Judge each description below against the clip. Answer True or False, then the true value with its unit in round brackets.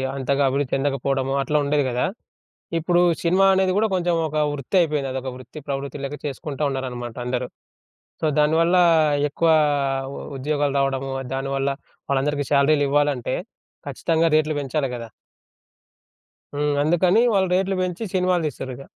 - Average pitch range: True (3.2 semitones)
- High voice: False (145 Hz)